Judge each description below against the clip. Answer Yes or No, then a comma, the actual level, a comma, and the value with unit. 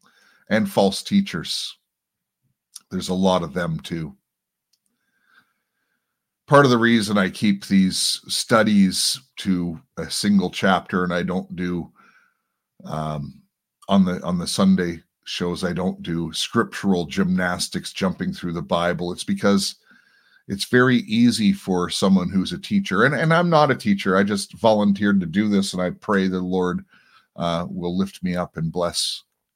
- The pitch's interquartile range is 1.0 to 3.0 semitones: Yes, narrow, 2.5 semitones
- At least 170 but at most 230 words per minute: No, average, 150 wpm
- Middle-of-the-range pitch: No, very low, 95 Hz